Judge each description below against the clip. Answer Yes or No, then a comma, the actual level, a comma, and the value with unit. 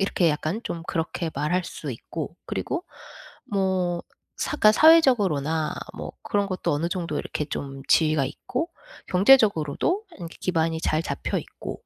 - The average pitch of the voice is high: No, medium, 175 Hz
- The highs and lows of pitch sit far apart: No, average, 4.5 semitones